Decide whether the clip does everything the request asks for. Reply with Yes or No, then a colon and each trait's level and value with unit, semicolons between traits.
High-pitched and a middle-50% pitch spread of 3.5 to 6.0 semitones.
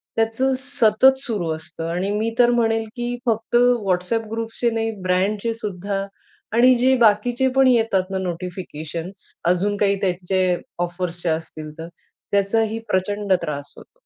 Yes: high, 205 Hz; average, 4.1 semitones